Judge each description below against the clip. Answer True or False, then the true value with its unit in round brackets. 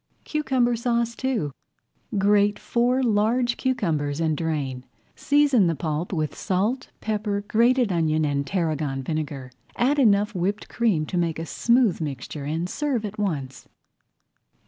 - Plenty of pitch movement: True (7.2 semitones)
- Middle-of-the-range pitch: False (200 Hz)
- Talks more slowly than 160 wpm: True (135 wpm)